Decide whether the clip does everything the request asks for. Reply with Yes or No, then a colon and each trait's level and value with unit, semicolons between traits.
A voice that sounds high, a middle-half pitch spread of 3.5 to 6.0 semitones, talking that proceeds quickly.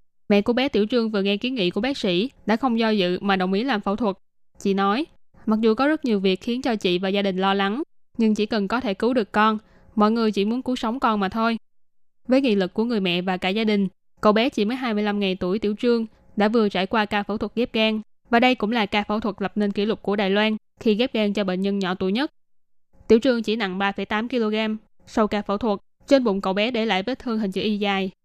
No: high, 210 Hz; narrow, 2.4 semitones; fast, 270 wpm